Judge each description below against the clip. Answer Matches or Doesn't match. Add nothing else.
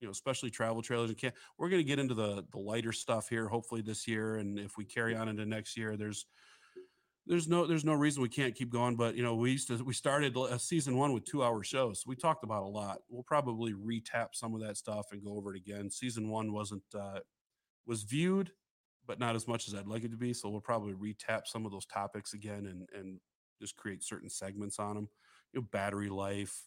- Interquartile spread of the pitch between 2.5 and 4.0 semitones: Matches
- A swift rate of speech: Matches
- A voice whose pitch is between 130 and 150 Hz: Doesn't match